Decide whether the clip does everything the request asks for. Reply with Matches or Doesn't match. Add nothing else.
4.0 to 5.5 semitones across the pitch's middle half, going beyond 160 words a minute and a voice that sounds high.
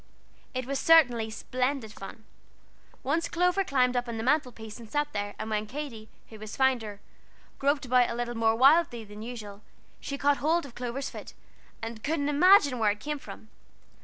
Matches